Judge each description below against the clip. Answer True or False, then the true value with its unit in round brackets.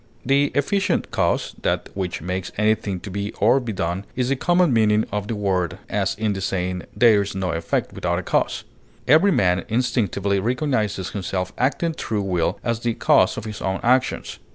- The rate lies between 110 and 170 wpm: False (185 wpm)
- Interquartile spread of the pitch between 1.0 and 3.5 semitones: False (4.5 semitones)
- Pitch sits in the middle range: False (105 Hz)